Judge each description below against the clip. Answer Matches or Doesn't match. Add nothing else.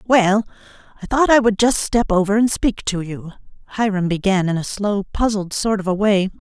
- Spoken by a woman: Matches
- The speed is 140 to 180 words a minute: Doesn't match